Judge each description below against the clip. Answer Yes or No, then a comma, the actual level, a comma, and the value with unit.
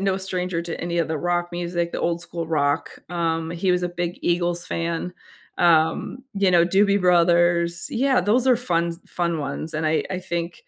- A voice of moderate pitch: Yes, medium, 175 Hz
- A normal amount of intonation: No, narrow, 1.3 semitones